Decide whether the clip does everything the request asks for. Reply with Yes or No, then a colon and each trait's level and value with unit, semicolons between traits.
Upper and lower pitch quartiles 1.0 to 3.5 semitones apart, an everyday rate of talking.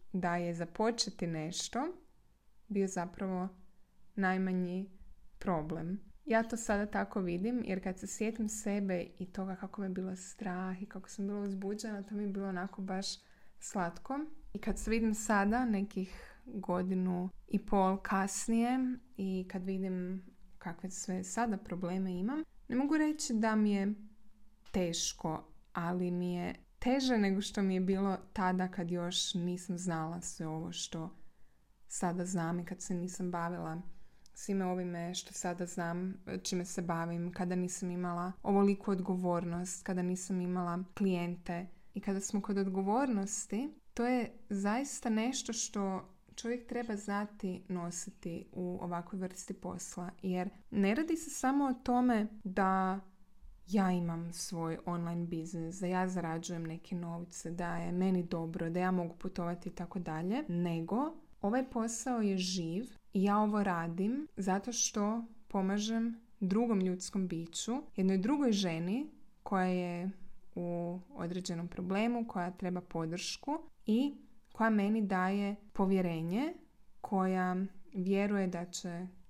Yes: average, 2.9 semitones; average, 140 wpm